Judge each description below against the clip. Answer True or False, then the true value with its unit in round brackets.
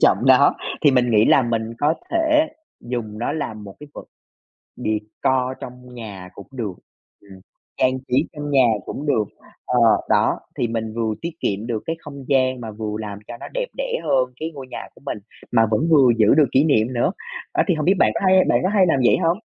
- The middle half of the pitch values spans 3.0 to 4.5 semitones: False (5.2 semitones)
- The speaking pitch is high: False (125 Hz)